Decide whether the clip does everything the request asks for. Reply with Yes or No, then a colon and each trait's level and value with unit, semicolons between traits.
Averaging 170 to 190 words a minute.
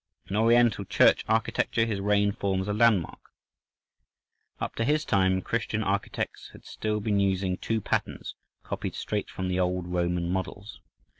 No: average, 145 wpm